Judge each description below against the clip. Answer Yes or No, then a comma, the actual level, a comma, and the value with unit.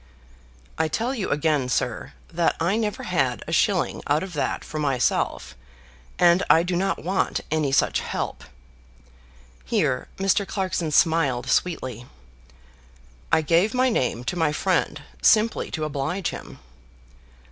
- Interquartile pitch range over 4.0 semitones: Yes, average, 5.2 semitones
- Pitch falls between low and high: Yes, medium, 165 Hz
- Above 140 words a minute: No, slow, 135 wpm